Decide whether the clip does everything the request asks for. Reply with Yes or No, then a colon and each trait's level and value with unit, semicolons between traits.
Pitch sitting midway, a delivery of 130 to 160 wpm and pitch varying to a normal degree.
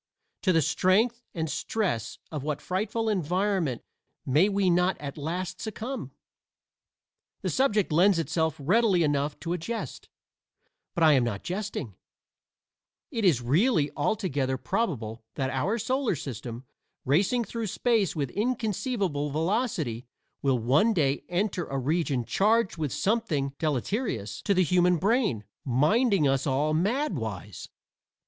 No: medium, 170 Hz; slow, 135 wpm; wide, 7.2 semitones